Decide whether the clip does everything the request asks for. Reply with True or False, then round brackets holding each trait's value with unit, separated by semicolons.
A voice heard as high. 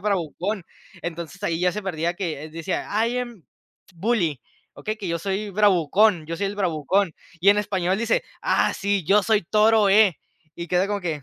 True (195 Hz)